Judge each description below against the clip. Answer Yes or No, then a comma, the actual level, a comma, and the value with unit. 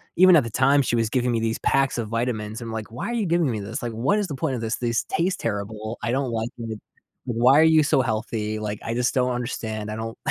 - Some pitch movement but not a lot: Yes, average, 3.0 semitones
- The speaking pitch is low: Yes, low, 115 Hz